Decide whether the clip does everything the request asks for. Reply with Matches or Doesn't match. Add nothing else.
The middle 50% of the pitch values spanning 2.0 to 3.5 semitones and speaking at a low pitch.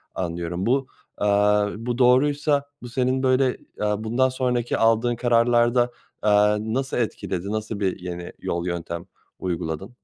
Doesn't match